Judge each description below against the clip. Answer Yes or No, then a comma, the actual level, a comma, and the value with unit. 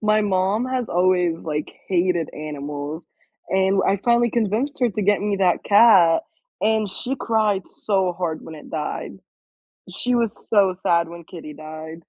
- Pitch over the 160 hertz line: Yes, high, 190 Hz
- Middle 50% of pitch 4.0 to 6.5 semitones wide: Yes, average, 4.5 semitones